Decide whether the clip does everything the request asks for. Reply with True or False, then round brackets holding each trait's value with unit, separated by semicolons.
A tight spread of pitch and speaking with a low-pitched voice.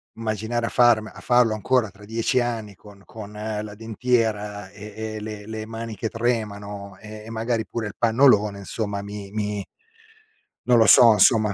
True (1.8 semitones; 110 Hz)